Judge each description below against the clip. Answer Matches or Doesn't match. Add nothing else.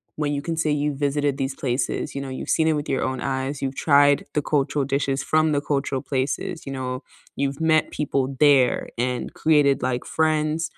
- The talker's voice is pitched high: Doesn't match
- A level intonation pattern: Matches